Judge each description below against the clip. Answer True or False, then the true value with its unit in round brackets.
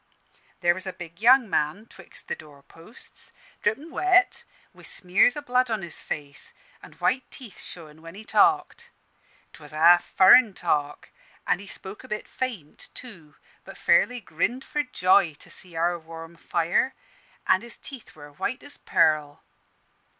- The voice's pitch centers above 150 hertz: True (185 Hz)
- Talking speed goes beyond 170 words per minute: False (160 wpm)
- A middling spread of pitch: False (7.1 semitones)